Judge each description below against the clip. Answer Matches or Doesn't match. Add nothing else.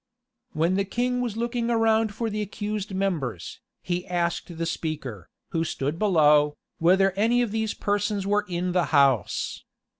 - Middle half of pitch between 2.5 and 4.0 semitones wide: Doesn't match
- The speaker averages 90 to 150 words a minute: Doesn't match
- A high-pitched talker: Matches